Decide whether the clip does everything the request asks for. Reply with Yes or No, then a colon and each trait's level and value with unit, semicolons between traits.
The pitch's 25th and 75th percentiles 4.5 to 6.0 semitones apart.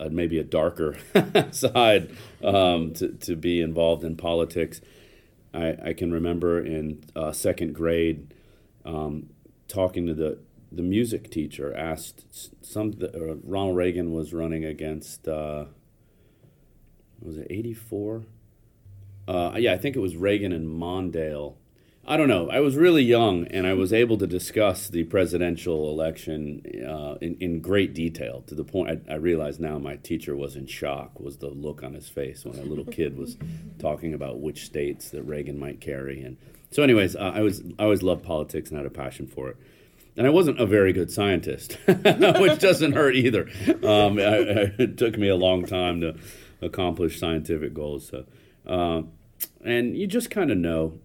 No: average, 3.7 semitones